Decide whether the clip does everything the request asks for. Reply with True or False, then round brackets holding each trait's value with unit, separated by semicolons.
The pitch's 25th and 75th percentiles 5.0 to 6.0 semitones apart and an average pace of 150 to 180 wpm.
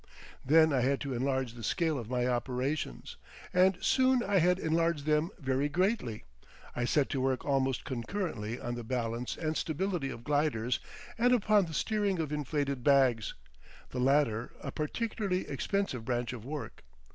True (5.3 semitones; 160 wpm)